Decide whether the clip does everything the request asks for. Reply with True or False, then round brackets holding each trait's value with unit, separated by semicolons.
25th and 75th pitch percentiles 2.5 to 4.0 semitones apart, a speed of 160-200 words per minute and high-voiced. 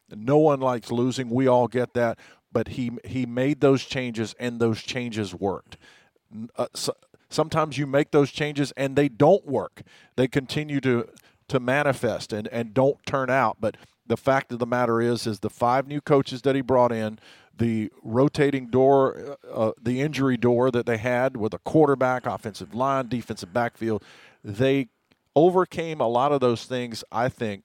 False (2.8 semitones; 180 wpm; 125 Hz)